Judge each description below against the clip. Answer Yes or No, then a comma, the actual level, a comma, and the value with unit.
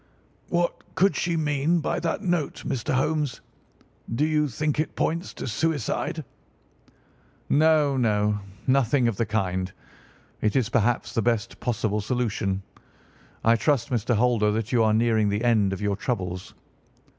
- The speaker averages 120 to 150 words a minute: Yes, average, 145 wpm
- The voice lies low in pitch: Yes, low, 120 Hz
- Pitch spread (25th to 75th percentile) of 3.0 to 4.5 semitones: No, wide, 5.6 semitones